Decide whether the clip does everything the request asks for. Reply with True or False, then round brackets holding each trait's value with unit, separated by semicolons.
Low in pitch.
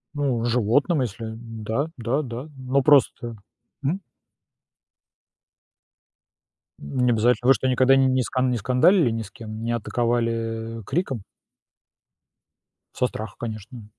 True (120 Hz)